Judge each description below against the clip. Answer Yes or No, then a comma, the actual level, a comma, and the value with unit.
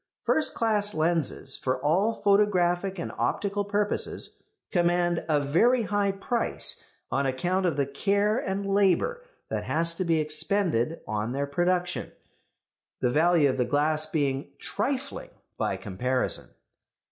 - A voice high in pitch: No, medium, 175 Hz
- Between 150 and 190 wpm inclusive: No, slow, 135 wpm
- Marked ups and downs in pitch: Yes, wide, 5.8 semitones